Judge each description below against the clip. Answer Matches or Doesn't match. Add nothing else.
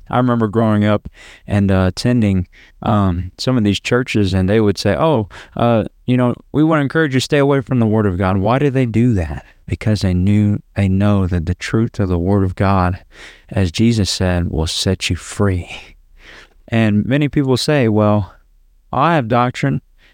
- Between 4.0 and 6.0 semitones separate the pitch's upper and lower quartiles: Matches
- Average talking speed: Matches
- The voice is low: Matches